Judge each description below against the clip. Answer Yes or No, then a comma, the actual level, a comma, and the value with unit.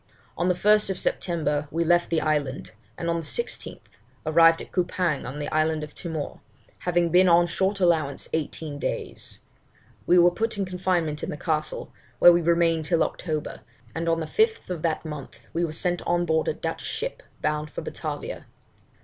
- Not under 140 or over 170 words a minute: No, average, 180 wpm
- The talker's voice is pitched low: No, medium, 170 Hz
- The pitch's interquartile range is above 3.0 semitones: No, narrow, 2.4 semitones